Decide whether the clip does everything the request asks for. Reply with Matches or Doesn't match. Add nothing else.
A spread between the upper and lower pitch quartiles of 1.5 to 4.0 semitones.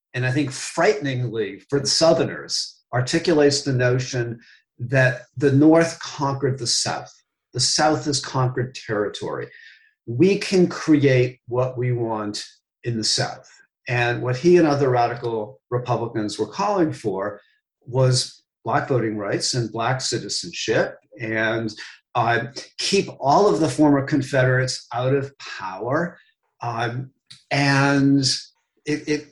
Matches